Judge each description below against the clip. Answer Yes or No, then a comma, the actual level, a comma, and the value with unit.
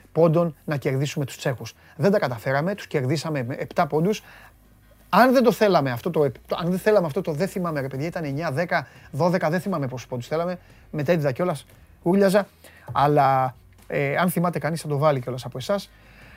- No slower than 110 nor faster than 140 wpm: No, fast, 170 wpm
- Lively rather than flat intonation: No, average, 4.7 semitones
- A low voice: No, medium, 155 Hz